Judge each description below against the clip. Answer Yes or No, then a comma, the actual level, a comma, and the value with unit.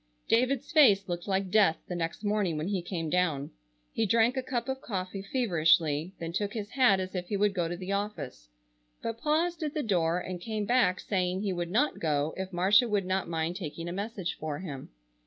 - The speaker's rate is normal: No, fast, 210 wpm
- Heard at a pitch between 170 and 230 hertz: Yes, high, 190 Hz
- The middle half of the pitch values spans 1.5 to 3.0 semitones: No, average, 4.0 semitones